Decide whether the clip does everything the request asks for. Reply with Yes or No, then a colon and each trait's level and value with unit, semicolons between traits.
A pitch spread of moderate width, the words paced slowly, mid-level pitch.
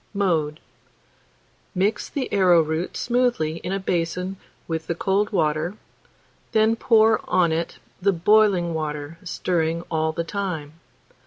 Yes: average, 3.8 semitones; slow, 120 wpm; medium, 175 Hz